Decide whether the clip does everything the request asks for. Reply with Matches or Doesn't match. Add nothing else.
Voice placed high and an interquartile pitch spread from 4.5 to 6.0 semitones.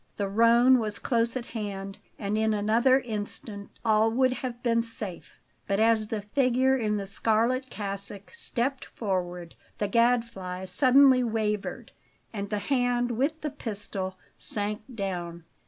Doesn't match